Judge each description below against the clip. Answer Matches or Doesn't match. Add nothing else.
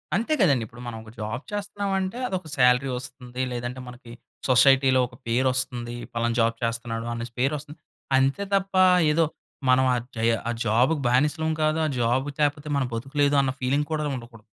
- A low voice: Matches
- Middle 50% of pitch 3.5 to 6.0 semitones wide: Matches